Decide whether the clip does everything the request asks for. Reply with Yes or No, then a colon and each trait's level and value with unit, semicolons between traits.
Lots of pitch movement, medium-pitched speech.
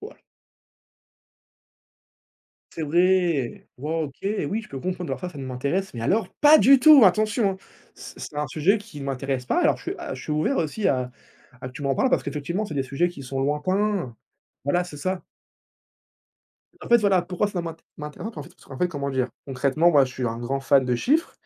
Yes: wide, 5.7 semitones; medium, 155 Hz